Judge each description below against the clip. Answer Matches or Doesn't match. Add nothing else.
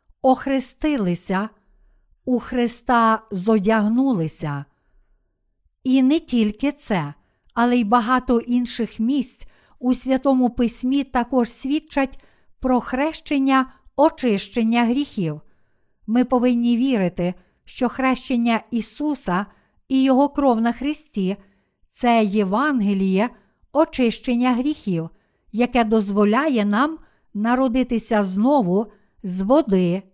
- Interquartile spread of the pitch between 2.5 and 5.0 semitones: Matches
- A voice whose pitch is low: Doesn't match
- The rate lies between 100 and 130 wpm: Doesn't match